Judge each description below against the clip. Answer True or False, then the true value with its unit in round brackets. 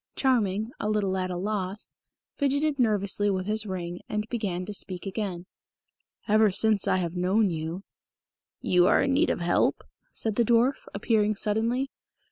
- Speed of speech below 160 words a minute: False (165 wpm)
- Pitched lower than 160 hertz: False (205 Hz)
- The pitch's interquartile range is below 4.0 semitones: True (3.2 semitones)